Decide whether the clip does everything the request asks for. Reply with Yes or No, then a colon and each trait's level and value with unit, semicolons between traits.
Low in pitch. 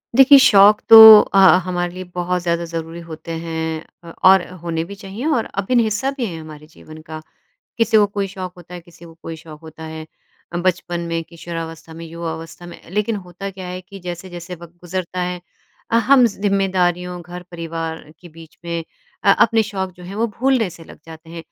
No: medium, 175 Hz